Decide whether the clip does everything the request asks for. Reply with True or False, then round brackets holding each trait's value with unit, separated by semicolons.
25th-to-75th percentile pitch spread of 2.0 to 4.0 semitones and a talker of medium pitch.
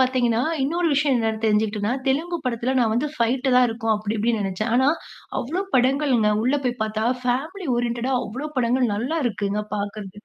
False (3.4 semitones; 240 Hz)